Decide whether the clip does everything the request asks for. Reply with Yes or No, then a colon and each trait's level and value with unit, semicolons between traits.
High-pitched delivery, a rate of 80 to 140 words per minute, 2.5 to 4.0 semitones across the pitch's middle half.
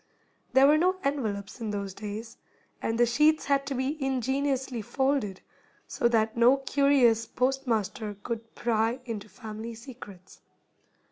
Yes: high, 240 Hz; slow, 135 wpm; average, 3.7 semitones